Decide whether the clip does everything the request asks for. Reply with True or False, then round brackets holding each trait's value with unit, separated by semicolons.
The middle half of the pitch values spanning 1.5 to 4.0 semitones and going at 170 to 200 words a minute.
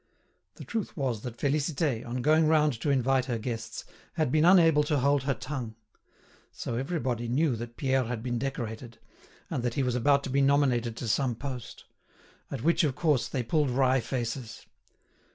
True (3.3 semitones; 180 wpm)